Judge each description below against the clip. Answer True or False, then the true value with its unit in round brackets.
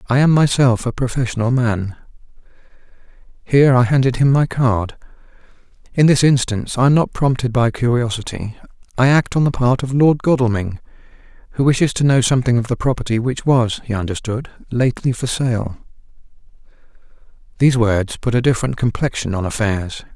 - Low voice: True (125 Hz)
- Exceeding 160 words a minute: False (155 wpm)